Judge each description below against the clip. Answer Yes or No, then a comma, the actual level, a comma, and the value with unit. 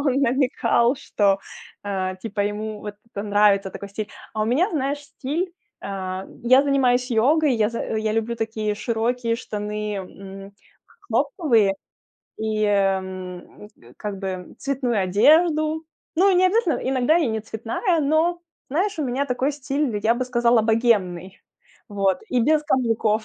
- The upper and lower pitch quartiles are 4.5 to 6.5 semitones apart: Yes, average, 5.2 semitones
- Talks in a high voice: Yes, high, 230 Hz